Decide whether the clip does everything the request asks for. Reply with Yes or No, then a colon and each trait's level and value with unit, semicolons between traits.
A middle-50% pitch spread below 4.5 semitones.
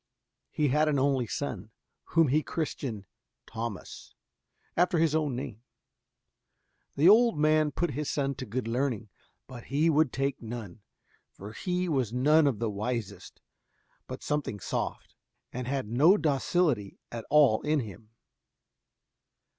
No: average, 5.0 semitones